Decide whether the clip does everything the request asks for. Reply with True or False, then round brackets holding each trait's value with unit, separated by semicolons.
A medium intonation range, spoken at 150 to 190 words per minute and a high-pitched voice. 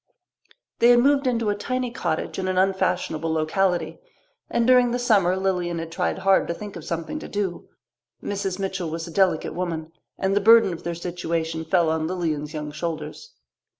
False (3.8 semitones; 185 wpm; 180 Hz)